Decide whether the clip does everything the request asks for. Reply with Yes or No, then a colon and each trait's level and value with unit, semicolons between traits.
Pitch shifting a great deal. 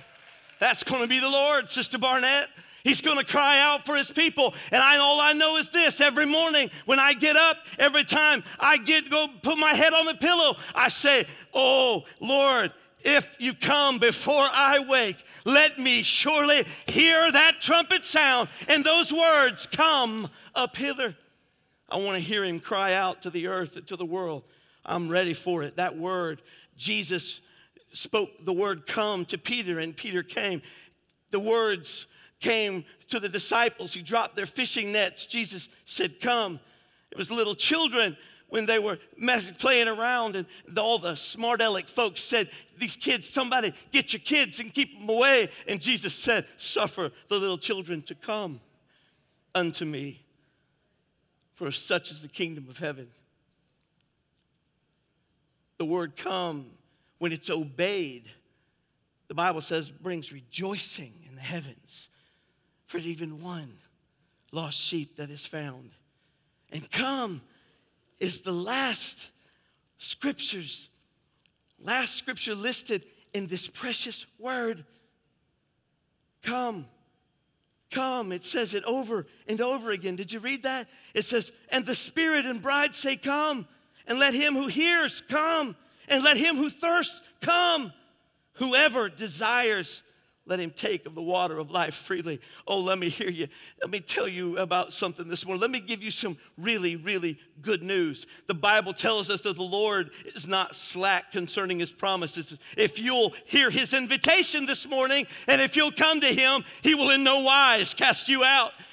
Yes: wide, 7.3 semitones